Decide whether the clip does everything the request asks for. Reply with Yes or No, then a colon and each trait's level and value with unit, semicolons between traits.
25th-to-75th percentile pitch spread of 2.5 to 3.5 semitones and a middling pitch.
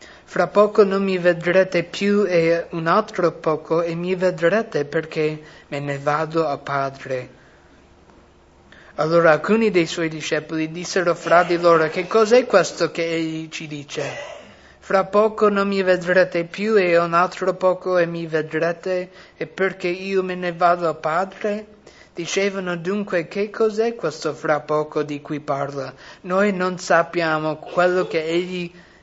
Yes: average, 2.9 semitones; medium, 175 Hz